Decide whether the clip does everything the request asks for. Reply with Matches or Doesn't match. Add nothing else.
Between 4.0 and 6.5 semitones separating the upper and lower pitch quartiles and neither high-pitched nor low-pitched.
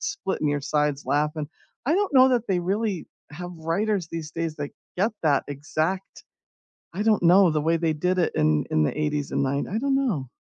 Matches